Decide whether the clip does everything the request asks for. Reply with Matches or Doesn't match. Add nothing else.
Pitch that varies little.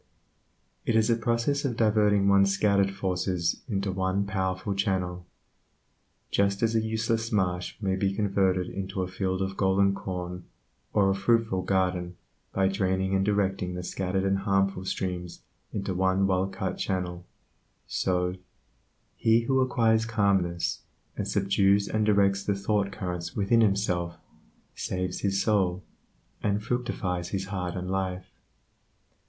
Matches